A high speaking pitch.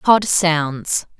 No: medium, 165 Hz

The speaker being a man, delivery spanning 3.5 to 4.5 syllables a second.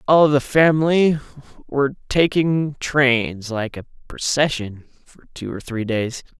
Yes: male; 4.0 syllables/s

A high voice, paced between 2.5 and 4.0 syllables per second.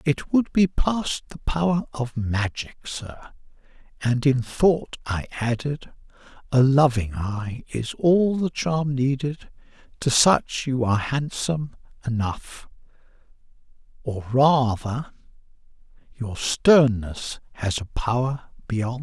No: low, 130 Hz; 3.8 syllables/s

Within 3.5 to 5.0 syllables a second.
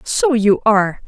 Yes: 4.4 syllables/s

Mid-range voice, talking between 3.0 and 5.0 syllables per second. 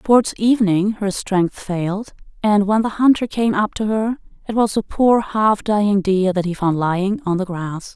No: high, 205 Hz; 4.7 syllables/s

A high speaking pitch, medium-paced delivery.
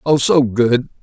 No: low, 125 Hz; average, 175 wpm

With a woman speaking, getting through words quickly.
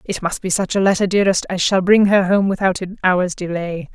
Yes: female; fast, 245 wpm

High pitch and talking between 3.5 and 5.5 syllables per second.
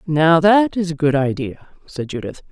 No: medium, 160 Hz; 4.7 syllables/s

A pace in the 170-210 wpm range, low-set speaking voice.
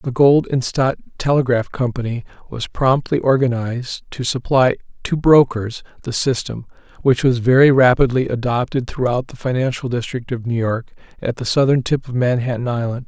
No: average, 155 wpm; low, 125 Hz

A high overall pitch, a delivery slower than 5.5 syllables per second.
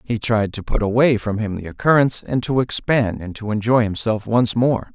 No: low, 115 Hz; 5.2 syllables/s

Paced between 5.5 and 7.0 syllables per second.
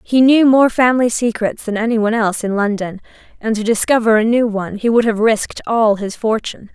Yes: 6.0 syllables/s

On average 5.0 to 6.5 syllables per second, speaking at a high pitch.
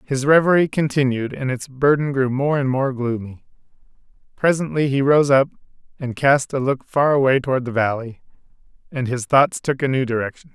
No: 5.3 syllables/s; low, 135 Hz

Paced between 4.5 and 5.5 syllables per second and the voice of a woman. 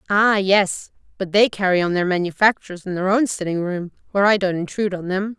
No: 5.9 syllables/s; female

